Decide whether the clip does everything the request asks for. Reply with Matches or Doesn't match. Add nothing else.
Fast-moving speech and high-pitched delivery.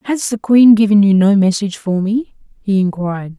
Doesn't match